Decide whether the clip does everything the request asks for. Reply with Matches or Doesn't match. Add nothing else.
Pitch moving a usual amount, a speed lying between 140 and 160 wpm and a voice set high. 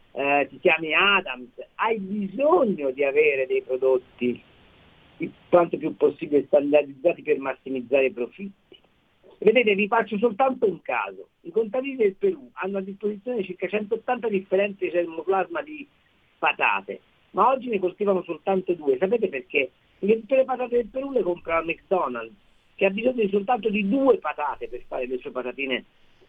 Doesn't match